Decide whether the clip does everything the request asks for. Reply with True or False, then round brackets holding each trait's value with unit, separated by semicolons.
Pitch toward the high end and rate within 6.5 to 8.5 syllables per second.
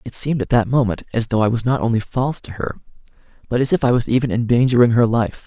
False (120 Hz; 6.7 syllables/s)